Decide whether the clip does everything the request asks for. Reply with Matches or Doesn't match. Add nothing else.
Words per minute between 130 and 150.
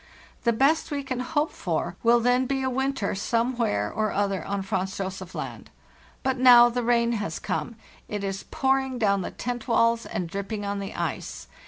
Doesn't match